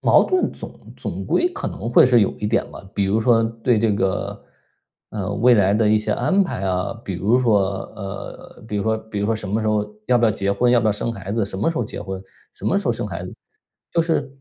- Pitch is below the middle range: Yes, low, 110 Hz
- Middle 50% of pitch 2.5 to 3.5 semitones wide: Yes, average, 2.8 semitones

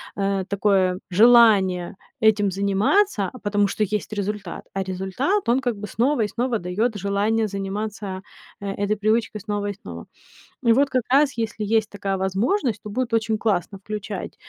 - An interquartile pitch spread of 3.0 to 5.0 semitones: No, narrow, 2.5 semitones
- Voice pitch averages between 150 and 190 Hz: No, high, 210 Hz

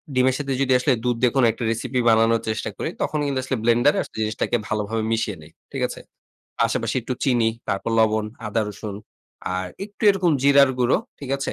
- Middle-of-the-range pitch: No, low, 120 Hz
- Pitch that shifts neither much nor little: Yes, average, 3.4 semitones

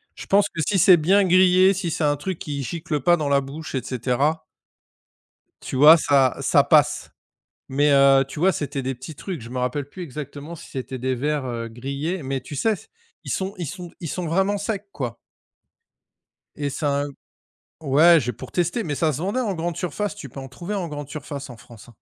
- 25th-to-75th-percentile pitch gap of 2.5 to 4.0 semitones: No, average, 4.6 semitones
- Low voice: No, medium, 150 Hz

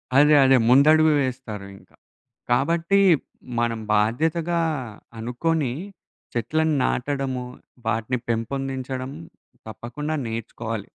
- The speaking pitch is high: No, low, 130 Hz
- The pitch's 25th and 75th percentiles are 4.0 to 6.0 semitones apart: Yes, average, 4.6 semitones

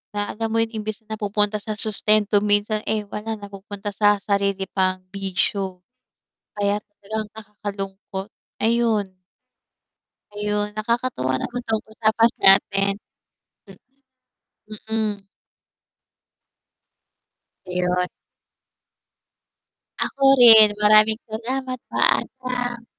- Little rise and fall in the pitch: Yes, narrow, 1.8 semitones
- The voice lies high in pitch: Yes, high, 210 Hz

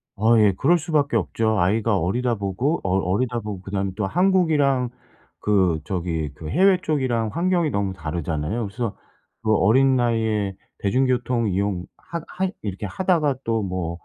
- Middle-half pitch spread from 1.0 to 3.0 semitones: No, wide, 5.6 semitones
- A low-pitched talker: Yes, low, 110 Hz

